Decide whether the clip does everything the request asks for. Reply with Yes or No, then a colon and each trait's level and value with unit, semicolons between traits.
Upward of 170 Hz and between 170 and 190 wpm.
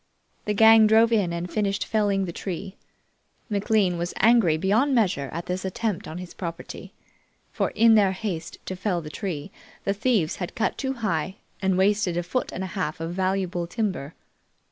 Yes: high, 190 Hz; average, 180 wpm